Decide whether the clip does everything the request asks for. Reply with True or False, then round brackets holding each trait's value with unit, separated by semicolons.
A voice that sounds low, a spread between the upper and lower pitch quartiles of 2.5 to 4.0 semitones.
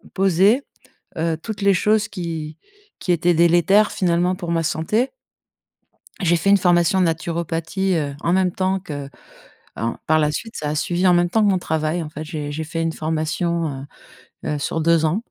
False (170 Hz; 2.9 semitones)